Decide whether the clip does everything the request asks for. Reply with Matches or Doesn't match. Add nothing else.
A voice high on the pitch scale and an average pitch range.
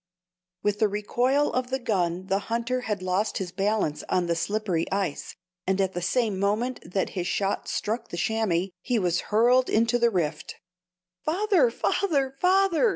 Matches